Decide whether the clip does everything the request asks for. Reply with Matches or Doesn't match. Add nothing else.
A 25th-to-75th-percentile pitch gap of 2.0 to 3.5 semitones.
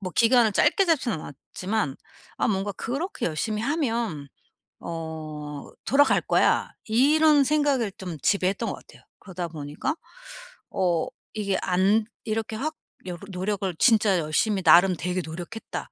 Doesn't match